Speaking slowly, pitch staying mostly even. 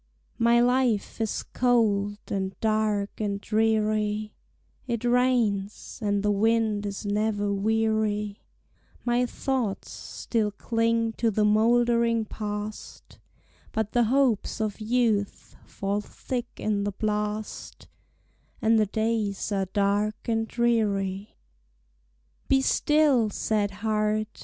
Yes: slow, 110 wpm; narrow, 2.0 semitones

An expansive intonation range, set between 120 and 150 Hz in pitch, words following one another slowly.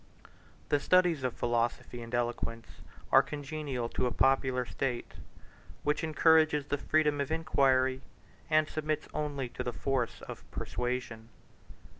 No: average, 3.7 semitones; low, 135 Hz; slow, 130 wpm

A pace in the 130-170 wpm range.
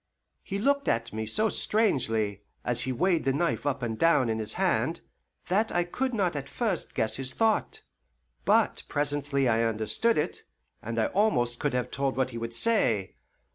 No: average, 180 wpm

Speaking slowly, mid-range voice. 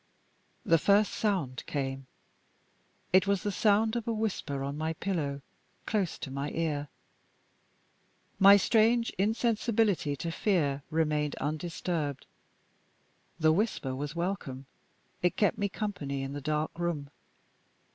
Yes: slow, 125 wpm; medium, 165 Hz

